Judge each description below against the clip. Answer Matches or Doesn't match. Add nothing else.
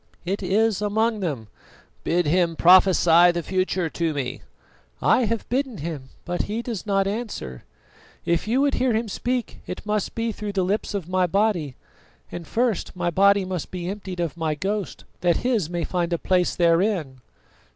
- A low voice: Doesn't match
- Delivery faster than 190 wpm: Doesn't match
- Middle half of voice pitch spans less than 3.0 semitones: Doesn't match